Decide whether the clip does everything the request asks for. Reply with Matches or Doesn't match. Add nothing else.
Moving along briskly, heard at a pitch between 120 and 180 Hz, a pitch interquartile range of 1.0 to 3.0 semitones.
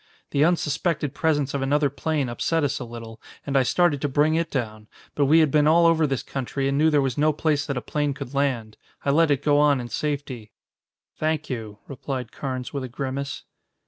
Matches